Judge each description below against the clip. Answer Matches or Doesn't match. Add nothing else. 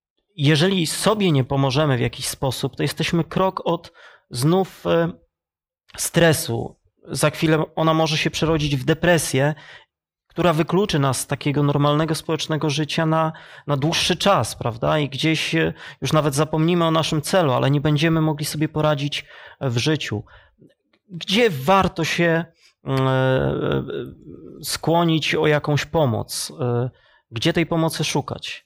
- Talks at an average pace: Matches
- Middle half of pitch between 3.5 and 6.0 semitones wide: Doesn't match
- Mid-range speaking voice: Matches